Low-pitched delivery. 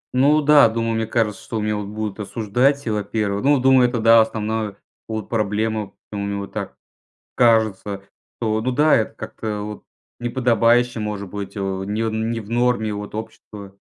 Yes: low, 110 Hz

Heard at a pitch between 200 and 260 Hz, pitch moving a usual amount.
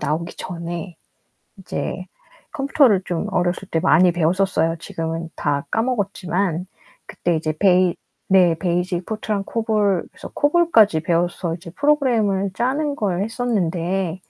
No: medium, 185 Hz; average, 4.1 semitones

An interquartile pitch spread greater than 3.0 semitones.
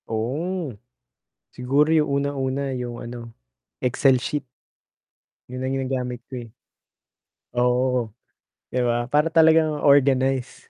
No: narrow, 2.5 semitones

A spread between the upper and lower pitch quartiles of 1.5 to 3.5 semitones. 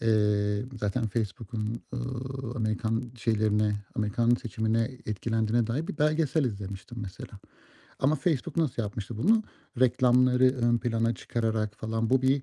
Yes: average, 2.9 semitones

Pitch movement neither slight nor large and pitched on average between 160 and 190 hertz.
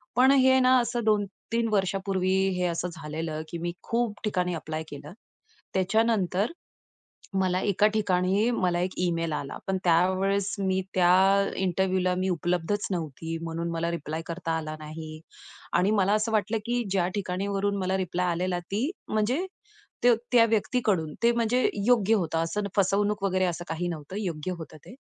Yes: average, 3.5 semitones; medium, 185 Hz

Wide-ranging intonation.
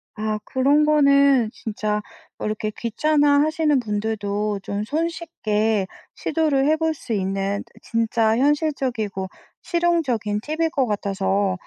Yes: wide, 6.1 semitones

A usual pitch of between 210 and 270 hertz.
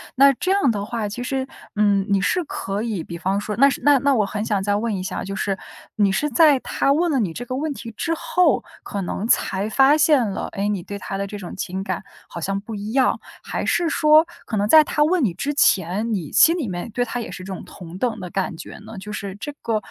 Yes: high, 215 Hz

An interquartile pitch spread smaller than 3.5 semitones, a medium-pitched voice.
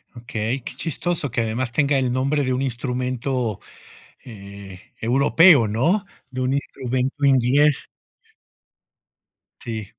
No: average, 2.9 semitones; low, 130 Hz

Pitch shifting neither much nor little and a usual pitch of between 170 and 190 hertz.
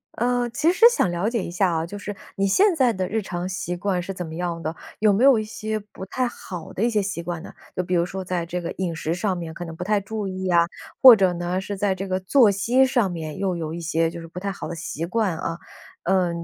Yes: average, 3.5 semitones; medium, 185 Hz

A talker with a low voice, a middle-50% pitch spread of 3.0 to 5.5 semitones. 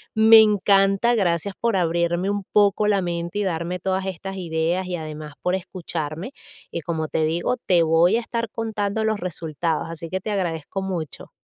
No: medium, 185 Hz; average, 3.4 semitones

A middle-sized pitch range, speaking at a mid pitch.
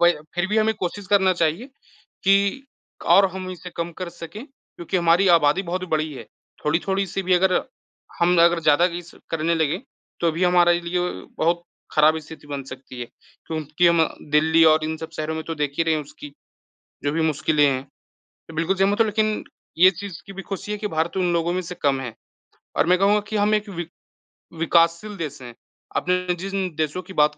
Yes: average, 3.3 semitones; medium, 170 Hz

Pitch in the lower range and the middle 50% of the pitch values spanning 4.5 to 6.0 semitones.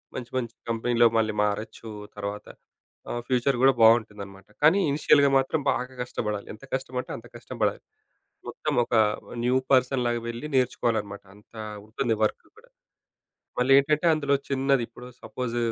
No: low, 120 Hz; average, 3.2 semitones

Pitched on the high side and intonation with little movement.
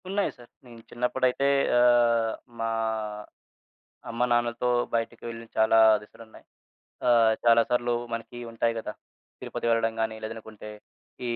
No: low, 115 Hz; narrow, 1.1 semitones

